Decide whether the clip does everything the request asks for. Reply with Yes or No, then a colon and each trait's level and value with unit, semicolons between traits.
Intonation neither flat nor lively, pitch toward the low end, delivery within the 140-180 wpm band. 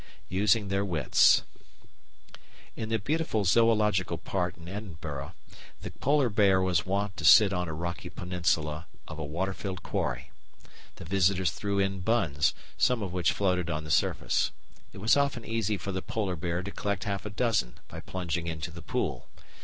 Yes: average, 3.4 semitones; very low, 95 Hz; average, 170 wpm